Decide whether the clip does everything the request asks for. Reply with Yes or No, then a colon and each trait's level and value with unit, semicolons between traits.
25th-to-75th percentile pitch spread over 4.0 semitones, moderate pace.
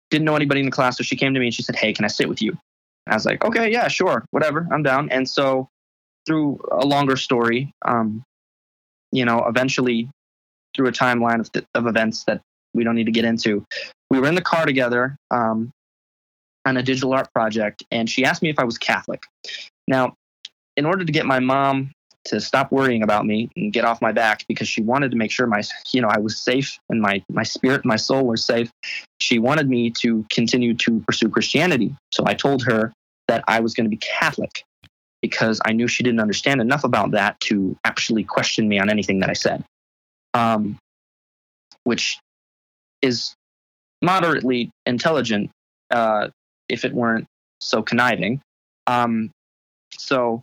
No: average, 3.1 semitones; average, 195 wpm